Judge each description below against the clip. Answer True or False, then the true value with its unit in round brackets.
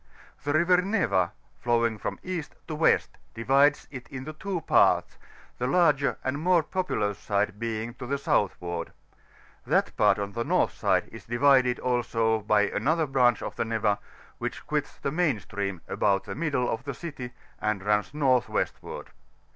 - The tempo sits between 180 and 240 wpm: False (165 wpm)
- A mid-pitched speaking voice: False (125 Hz)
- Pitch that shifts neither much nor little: False (5.7 semitones)